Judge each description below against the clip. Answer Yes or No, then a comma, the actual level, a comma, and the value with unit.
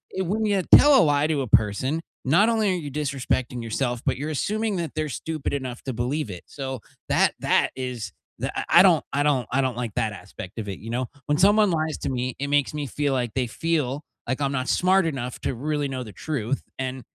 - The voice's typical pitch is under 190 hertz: Yes, low, 135 Hz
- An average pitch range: Yes, average, 4.0 semitones